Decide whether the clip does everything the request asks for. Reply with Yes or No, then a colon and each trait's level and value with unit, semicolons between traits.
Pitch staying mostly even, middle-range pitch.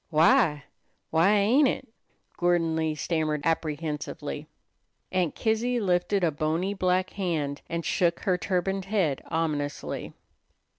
No: average, 3.5 semitones; medium, 175 Hz